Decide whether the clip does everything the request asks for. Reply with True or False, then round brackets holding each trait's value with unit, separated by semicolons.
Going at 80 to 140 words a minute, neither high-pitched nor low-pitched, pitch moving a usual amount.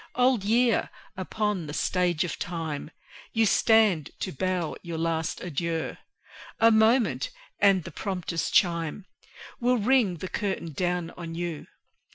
True (135 wpm; 180 Hz; 4.7 semitones)